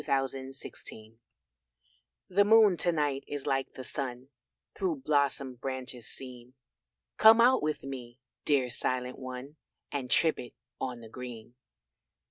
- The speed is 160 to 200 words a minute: No, slow, 135 wpm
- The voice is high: No, low, 135 Hz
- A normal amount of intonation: Yes, average, 3.0 semitones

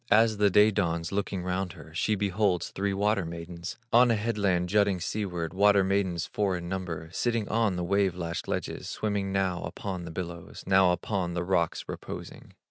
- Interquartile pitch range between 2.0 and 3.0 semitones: Yes, average, 2.7 semitones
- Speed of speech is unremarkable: Yes, average, 180 wpm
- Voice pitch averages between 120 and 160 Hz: No, very low, 95 Hz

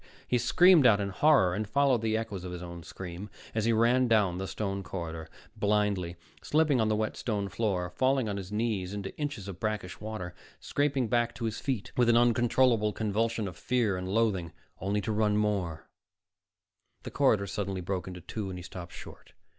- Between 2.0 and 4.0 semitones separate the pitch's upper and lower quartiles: Yes, average, 3.7 semitones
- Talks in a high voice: No, low, 105 Hz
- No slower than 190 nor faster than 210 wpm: Yes, average, 195 wpm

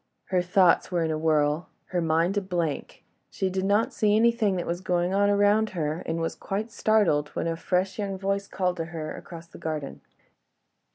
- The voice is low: No, medium, 180 Hz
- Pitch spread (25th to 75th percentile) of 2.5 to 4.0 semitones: Yes, average, 3.4 semitones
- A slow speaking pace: No, average, 190 wpm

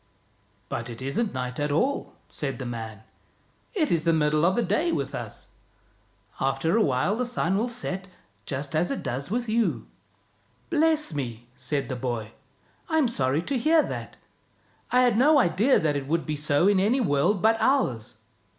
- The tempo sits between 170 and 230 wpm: Yes, average, 190 wpm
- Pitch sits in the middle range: Yes, medium, 165 Hz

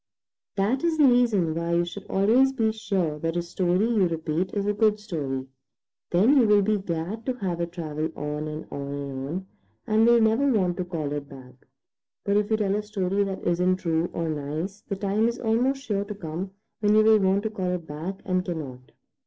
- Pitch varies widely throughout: No, average, 4.7 semitones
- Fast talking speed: Yes, fast, 215 wpm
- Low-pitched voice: No, high, 190 Hz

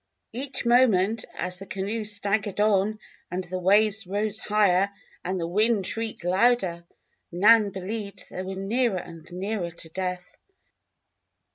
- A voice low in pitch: No, high, 200 Hz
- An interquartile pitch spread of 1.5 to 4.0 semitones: Yes, average, 2.9 semitones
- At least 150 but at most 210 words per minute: No, average, 140 wpm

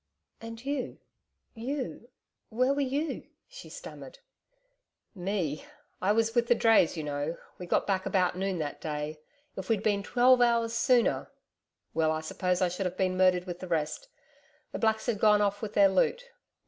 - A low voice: No, high, 200 Hz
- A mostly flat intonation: No, average, 4.8 semitones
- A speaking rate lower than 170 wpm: No, average, 175 wpm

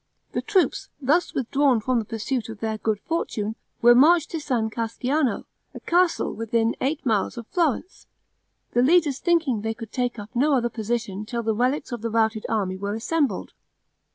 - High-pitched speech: Yes, high, 240 Hz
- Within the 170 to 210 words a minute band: Yes, average, 180 wpm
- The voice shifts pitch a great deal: No, average, 4.3 semitones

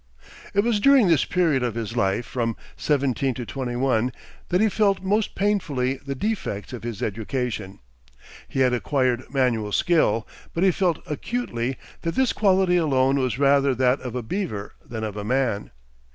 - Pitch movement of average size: No, wide, 6.9 semitones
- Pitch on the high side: No, low, 130 Hz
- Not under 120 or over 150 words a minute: No, average, 170 wpm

